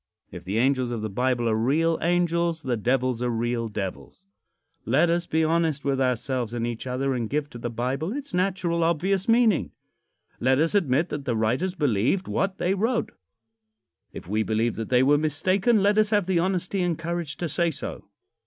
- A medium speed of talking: Yes, average, 190 wpm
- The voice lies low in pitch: No, medium, 145 Hz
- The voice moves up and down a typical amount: No, wide, 6.5 semitones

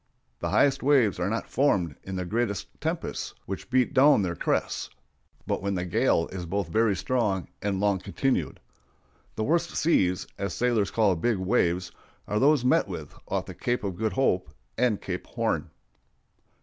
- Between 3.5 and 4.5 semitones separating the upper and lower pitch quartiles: No, average, 5.0 semitones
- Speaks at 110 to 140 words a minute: No, average, 170 wpm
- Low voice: Yes, low, 105 Hz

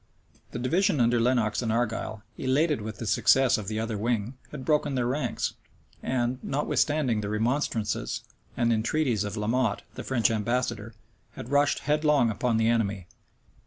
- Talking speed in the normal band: Yes, average, 160 wpm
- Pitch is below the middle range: Yes, low, 120 Hz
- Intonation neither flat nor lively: Yes, average, 3.3 semitones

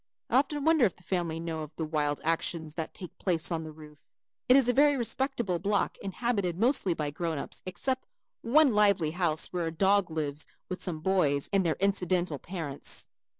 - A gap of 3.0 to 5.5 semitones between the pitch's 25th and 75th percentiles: Yes, average, 4.7 semitones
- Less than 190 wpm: No, average, 195 wpm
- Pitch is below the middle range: No, medium, 180 Hz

